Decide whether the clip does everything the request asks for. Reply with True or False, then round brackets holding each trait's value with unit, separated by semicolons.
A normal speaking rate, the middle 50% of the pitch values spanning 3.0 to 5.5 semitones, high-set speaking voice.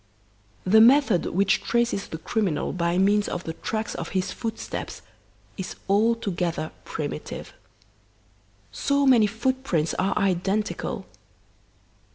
False (110 wpm; 3.9 semitones; 200 Hz)